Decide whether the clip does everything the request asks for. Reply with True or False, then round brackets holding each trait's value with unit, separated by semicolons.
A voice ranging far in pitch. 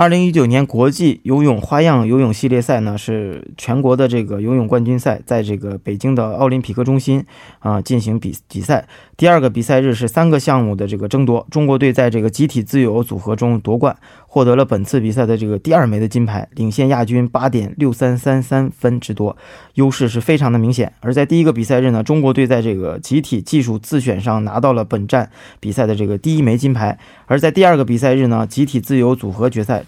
False (3.3 semitones)